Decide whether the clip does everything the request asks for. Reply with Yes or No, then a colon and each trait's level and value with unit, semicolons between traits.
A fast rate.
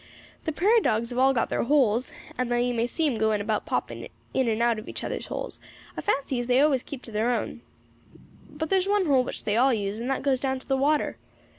Yes: fast, 250 wpm